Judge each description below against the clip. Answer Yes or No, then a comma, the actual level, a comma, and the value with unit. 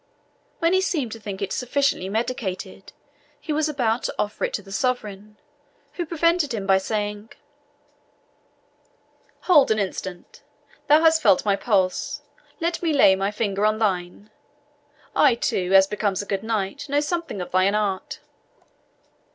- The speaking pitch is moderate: No, high, 215 Hz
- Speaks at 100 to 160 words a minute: Yes, average, 150 wpm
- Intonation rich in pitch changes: Yes, wide, 6.6 semitones